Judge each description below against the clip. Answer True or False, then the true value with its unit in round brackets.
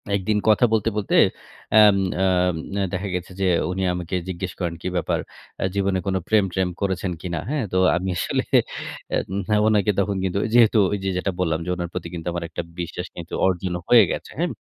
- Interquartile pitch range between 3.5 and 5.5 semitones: False (2.5 semitones)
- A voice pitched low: True (95 Hz)